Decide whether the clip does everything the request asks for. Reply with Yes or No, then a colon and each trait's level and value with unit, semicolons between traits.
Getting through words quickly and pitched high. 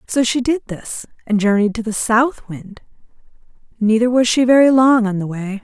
No: average, 190 wpm; high, 230 Hz